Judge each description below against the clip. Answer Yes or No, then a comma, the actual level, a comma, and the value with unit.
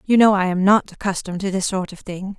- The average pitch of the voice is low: No, high, 195 Hz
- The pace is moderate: No, fast, 275 wpm